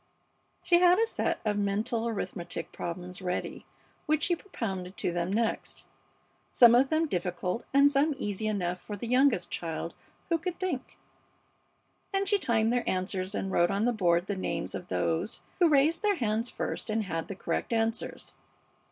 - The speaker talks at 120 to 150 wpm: No, average, 170 wpm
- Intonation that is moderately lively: No, wide, 7.3 semitones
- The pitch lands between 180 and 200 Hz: No, high, 220 Hz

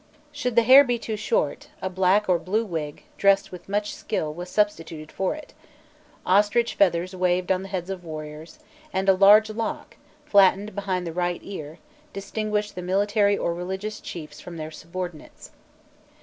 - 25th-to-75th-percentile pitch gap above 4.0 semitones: No, average, 2.9 semitones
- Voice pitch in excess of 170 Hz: Yes, high, 190 Hz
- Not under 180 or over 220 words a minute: No, average, 165 wpm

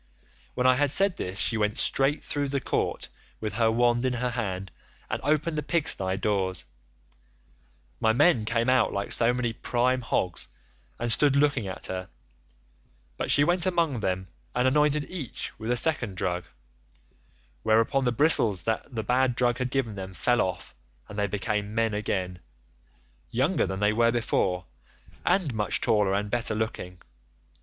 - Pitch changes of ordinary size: Yes, average, 4.2 semitones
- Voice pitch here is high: No, low, 115 Hz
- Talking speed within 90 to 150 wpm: No, average, 165 wpm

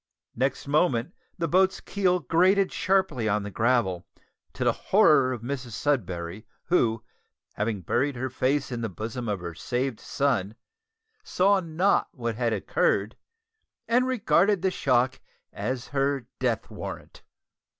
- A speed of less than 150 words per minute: Yes, average, 140 wpm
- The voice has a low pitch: Yes, low, 130 Hz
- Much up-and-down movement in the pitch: Yes, wide, 7.4 semitones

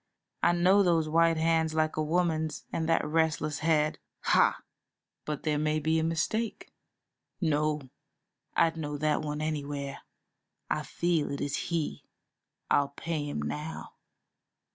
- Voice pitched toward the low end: No, medium, 155 Hz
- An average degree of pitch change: No, narrow, 1.8 semitones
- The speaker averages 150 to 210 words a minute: No, average, 140 wpm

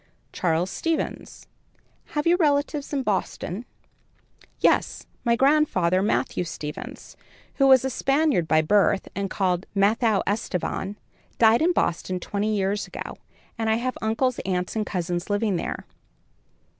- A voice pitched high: Yes, high, 210 Hz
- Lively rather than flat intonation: Yes, wide, 6.0 semitones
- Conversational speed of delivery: No, slow, 130 wpm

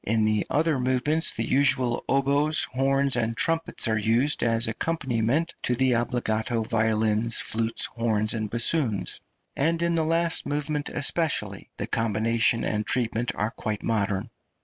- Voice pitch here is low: Yes, low, 120 Hz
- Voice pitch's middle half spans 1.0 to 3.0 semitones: No, average, 4.2 semitones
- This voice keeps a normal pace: Yes, average, 145 wpm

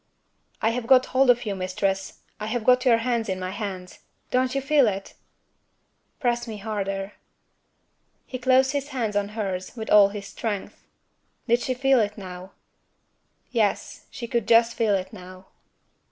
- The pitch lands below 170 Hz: No, high, 220 Hz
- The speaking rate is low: No, average, 165 wpm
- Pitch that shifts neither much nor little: Yes, average, 4.0 semitones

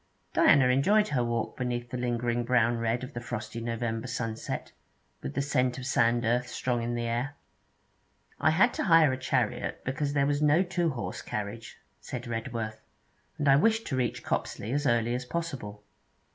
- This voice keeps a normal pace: Yes, average, 180 wpm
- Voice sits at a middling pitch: No, low, 125 Hz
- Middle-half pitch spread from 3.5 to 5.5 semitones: No, average, 3.1 semitones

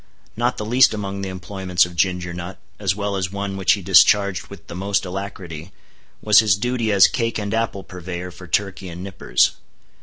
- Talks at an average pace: Yes, average, 190 wpm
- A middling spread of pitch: No, narrow, 2.1 semitones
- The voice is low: Yes, very low, 95 Hz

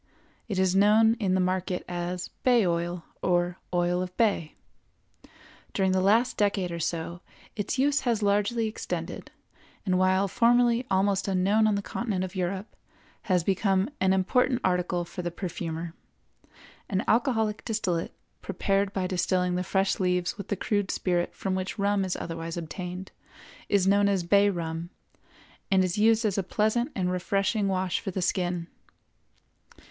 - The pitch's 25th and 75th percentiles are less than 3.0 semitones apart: Yes, narrow, 2.4 semitones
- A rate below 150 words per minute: No, average, 155 wpm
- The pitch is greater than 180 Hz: Yes, high, 190 Hz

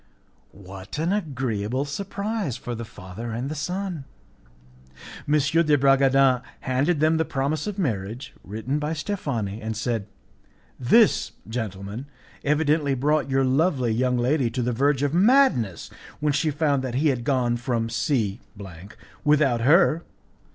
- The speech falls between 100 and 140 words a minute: Yes, slow, 135 wpm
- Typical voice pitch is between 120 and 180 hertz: Yes, low, 135 Hz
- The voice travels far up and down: No, average, 4.5 semitones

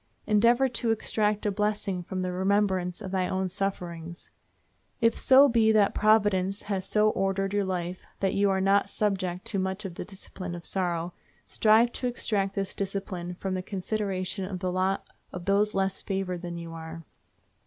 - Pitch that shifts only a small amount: Yes, narrow, 2.2 semitones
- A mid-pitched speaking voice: No, high, 195 Hz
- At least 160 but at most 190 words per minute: Yes, average, 175 wpm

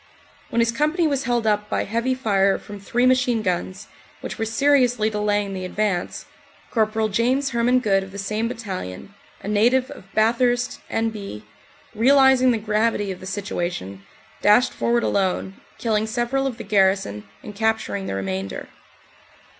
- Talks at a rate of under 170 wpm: Yes, average, 155 wpm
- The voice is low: No, high, 220 Hz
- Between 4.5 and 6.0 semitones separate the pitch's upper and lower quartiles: No, average, 3.7 semitones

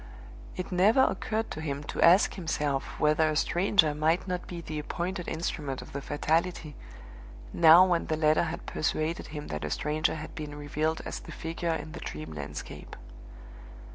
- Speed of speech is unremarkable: Yes, average, 170 wpm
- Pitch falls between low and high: Yes, medium, 155 Hz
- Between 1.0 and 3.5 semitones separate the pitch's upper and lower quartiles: Yes, average, 2.7 semitones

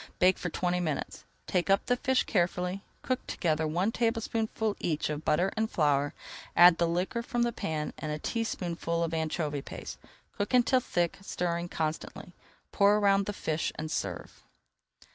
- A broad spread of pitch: No, average, 4.6 semitones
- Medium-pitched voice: Yes, medium, 180 Hz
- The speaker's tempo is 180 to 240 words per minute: No, average, 160 wpm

